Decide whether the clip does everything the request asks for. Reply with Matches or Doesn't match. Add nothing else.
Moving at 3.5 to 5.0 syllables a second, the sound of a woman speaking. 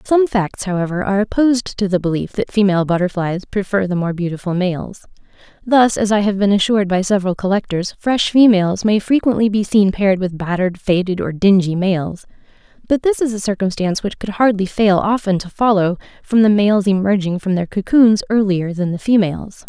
Doesn't match